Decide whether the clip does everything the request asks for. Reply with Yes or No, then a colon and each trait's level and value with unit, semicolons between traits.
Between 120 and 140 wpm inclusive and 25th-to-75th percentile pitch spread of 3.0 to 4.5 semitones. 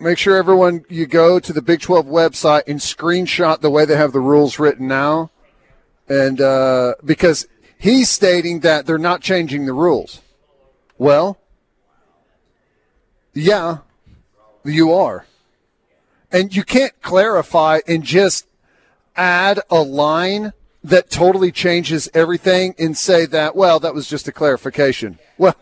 Yes: slow, 135 wpm; average, 3.6 semitones